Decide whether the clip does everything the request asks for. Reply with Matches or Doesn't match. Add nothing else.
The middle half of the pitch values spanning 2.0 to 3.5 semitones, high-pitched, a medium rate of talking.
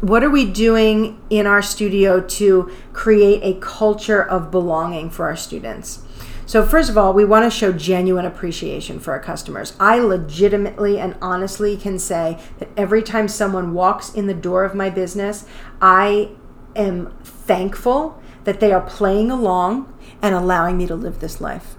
Matches